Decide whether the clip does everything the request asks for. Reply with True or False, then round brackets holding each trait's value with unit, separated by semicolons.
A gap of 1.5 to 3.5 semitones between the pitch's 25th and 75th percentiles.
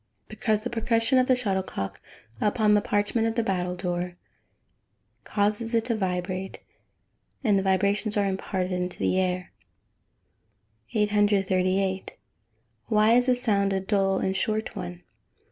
True (2.6 semitones)